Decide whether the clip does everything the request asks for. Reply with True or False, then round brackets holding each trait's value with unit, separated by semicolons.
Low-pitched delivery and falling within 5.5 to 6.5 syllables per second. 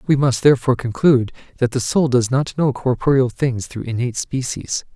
True (130 Hz; 5.6 syllables/s)